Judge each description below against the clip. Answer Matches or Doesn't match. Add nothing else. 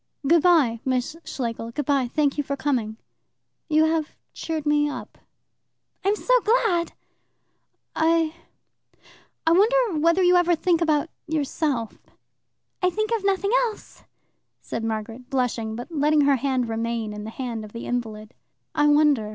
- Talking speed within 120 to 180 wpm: Matches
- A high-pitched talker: Matches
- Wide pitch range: Matches